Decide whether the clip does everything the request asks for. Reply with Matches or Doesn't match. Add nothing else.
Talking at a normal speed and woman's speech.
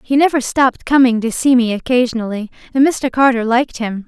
Matches